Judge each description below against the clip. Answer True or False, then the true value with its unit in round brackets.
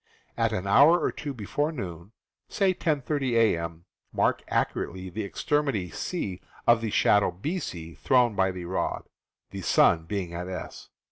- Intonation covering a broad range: True (7.7 semitones)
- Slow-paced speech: False (155 wpm)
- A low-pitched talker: True (105 Hz)